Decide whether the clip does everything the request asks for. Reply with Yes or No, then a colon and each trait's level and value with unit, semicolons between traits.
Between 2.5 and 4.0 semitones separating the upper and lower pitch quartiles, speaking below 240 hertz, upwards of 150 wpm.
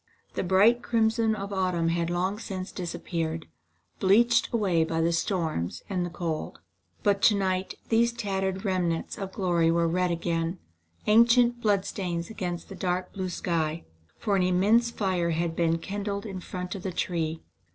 Yes: average, 3.1 semitones; medium, 185 Hz; average, 160 wpm